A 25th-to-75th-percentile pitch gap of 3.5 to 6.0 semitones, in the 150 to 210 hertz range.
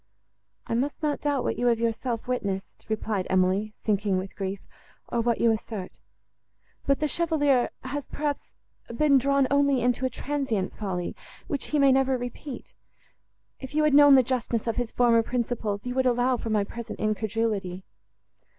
No: average, 4.2 semitones; high, 245 Hz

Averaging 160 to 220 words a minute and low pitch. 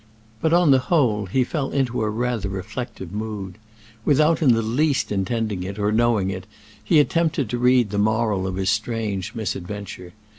Yes: average, 175 wpm; low, 110 Hz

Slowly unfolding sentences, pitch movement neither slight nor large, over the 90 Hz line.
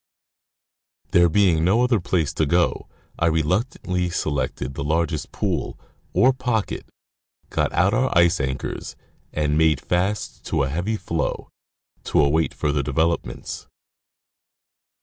No: slow, 125 wpm; average, 3.6 semitones; very low, 85 Hz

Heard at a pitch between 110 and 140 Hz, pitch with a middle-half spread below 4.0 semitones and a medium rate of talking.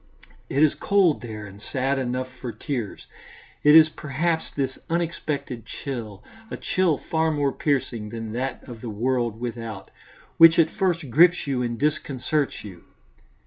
No: low, 135 Hz; average, 4.8 semitones; average, 150 wpm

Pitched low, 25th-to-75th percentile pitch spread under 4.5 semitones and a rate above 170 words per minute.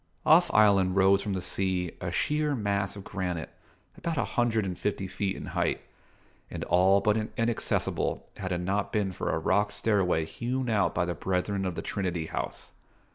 Yes: low, 100 Hz; narrow, 2.4 semitones; average, 185 wpm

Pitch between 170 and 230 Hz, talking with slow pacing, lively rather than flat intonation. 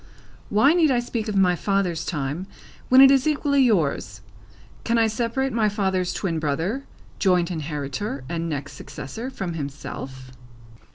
No: high, 190 Hz; average, 150 wpm; wide, 7.2 semitones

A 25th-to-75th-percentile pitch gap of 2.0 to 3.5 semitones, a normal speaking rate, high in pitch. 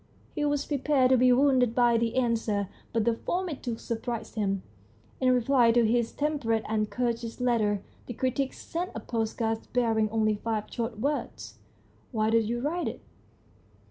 Yes: narrow, 2.5 semitones; average, 175 wpm; high, 235 Hz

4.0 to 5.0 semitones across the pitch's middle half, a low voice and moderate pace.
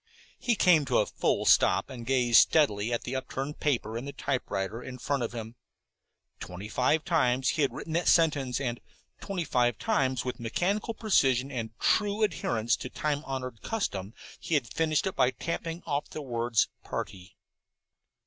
Yes: average, 4.7 semitones; low, 130 Hz; average, 170 wpm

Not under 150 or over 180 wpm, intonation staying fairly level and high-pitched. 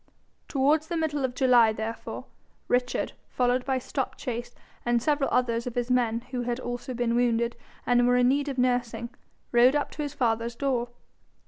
Yes: average, 175 wpm; narrow, 1.8 semitones; high, 245 Hz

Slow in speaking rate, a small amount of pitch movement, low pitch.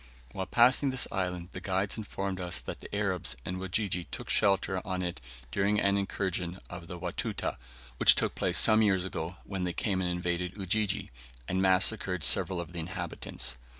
No: average, 180 wpm; narrow, 1.9 semitones; very low, 95 Hz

